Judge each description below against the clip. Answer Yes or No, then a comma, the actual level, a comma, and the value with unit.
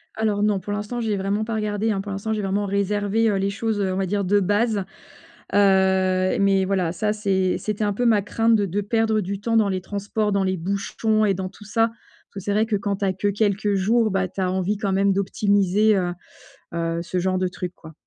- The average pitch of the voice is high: Yes, high, 200 Hz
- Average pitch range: No, narrow, 1.9 semitones